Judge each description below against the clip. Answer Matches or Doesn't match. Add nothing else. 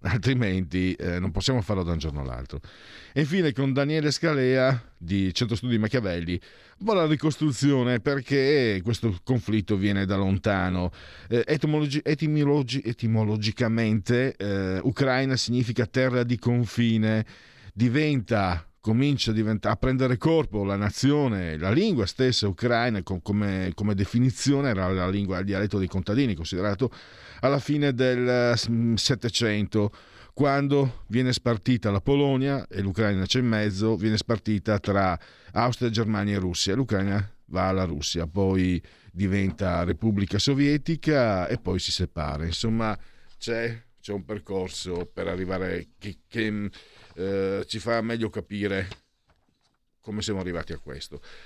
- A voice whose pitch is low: Matches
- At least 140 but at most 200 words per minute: Doesn't match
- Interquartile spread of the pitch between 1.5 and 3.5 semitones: Doesn't match